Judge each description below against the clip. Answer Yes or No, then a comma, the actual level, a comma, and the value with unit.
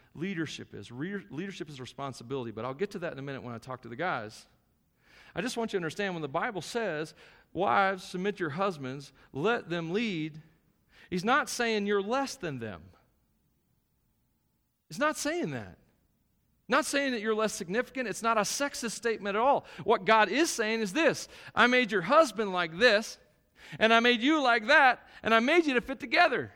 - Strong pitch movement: Yes, wide, 6.6 semitones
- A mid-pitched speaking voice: No, high, 205 Hz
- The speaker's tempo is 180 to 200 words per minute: Yes, average, 195 wpm